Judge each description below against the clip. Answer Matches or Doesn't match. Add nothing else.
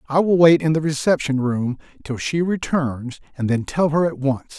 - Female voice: Doesn't match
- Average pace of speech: Doesn't match